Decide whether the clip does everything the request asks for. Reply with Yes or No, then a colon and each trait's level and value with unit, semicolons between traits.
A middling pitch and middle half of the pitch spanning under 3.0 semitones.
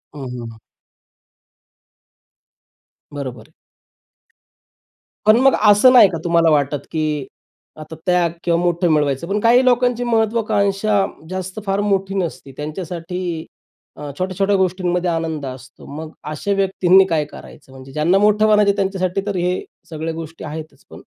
No: medium, 180 Hz; average, 4.3 semitones